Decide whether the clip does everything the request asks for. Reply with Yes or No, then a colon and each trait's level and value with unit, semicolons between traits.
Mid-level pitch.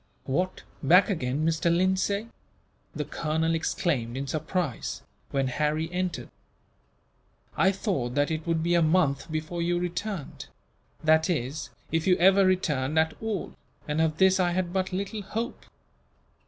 Yes: medium, 170 Hz